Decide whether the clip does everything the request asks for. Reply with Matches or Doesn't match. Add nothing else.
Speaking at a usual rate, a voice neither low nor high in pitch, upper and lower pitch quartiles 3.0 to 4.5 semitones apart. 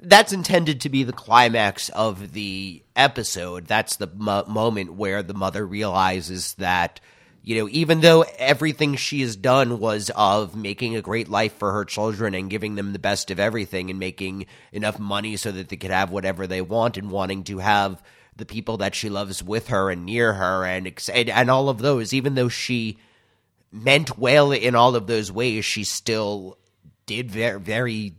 Doesn't match